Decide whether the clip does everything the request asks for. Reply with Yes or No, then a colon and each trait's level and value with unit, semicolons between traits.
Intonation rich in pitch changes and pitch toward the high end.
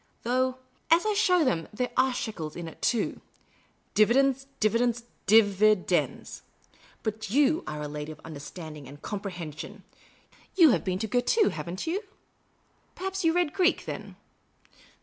Yes: wide, 7.8 semitones; high, 220 Hz